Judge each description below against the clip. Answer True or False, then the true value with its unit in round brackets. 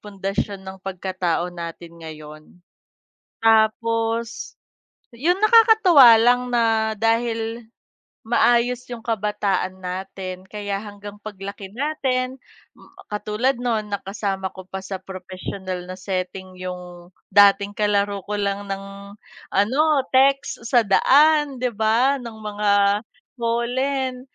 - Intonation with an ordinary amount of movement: True (3.9 semitones)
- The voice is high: True (210 Hz)